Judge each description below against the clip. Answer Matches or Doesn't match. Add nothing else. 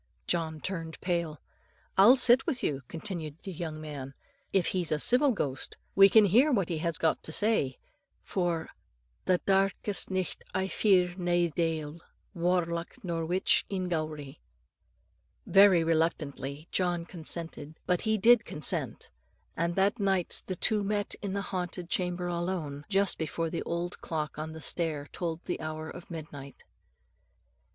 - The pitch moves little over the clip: Doesn't match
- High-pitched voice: Doesn't match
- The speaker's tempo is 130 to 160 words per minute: Matches